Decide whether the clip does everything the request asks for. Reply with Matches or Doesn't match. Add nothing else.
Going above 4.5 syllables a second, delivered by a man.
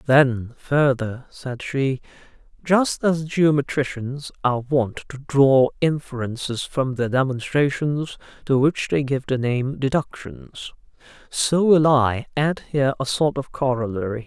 Doesn't match